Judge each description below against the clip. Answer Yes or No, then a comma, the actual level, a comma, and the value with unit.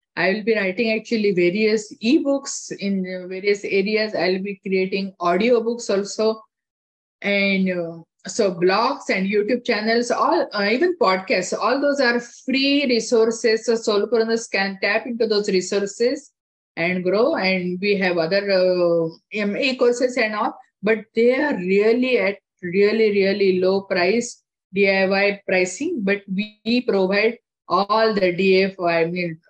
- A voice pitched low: No, high, 205 Hz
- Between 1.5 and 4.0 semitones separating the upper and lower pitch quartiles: Yes, average, 3.4 semitones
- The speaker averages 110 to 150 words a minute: Yes, average, 140 wpm